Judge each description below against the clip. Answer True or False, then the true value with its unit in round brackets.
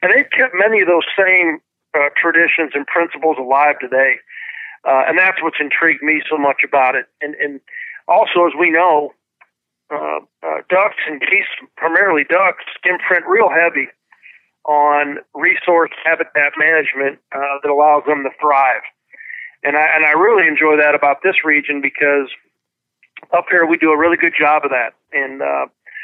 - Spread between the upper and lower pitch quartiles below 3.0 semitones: True (2.5 semitones)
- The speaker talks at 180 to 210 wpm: False (165 wpm)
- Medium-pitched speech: True (150 Hz)